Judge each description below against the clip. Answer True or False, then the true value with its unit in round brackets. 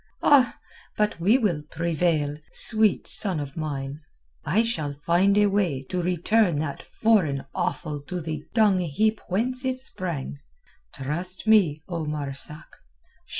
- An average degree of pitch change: False (5.9 semitones)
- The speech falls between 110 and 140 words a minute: True (135 wpm)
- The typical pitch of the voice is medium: True (175 Hz)